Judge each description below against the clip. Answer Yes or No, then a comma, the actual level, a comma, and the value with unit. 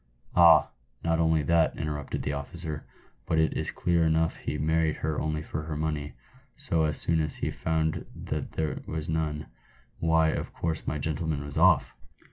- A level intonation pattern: Yes, narrow, 1.2 semitones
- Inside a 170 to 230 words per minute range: Yes, average, 175 wpm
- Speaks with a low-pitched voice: Yes, very low, 80 Hz